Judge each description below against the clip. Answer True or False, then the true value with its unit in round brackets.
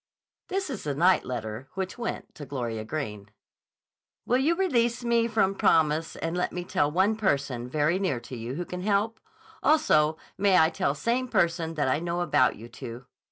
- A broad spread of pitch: True (7.0 semitones)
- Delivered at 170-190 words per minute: True (185 wpm)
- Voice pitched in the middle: True (170 Hz)